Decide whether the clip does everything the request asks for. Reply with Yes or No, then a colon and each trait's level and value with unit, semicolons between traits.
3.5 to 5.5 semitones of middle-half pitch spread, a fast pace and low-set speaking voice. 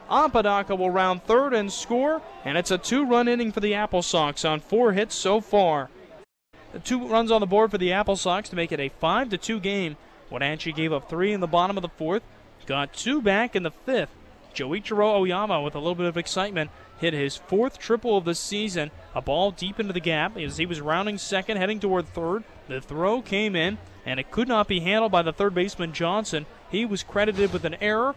No: average, 4.1 semitones; fast, 220 wpm; high, 190 Hz